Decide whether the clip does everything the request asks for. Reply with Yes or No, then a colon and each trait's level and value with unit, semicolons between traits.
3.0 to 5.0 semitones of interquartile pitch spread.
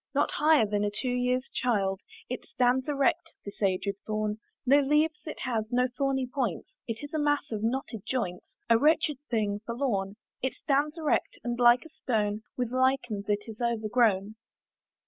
Yes: average, 4.3 semitones